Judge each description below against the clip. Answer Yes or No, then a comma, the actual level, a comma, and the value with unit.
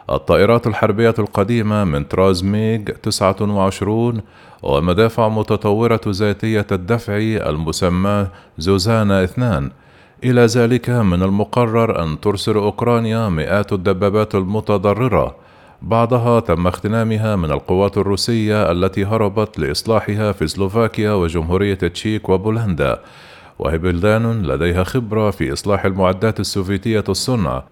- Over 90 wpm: Yes, average, 100 wpm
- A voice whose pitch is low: Yes, low, 105 Hz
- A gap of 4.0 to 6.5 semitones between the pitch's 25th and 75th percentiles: No, average, 2.7 semitones